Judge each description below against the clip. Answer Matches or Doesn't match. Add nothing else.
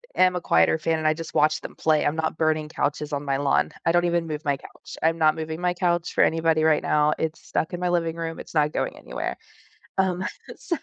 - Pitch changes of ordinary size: Doesn't match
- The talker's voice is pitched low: Doesn't match